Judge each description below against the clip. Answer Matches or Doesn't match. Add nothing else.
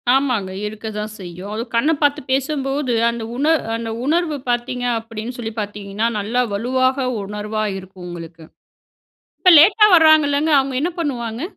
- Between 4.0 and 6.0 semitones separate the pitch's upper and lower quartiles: Matches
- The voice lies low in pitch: Doesn't match